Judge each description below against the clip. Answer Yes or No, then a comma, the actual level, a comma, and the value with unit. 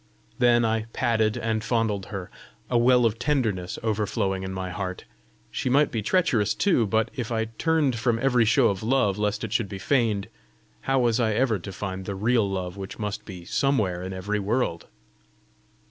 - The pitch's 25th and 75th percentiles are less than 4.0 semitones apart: Yes, average, 3.6 semitones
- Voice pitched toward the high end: No, low, 110 Hz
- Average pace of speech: Yes, average, 185 wpm